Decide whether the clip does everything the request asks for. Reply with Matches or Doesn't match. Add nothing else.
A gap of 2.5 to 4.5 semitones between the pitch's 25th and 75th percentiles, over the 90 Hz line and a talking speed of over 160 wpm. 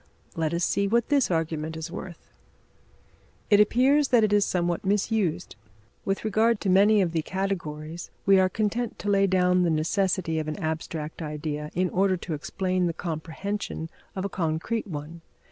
Matches